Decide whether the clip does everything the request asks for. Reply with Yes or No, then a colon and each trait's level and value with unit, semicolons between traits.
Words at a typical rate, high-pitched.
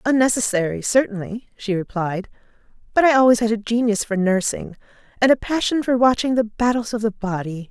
Yes: average, 170 wpm; high, 225 Hz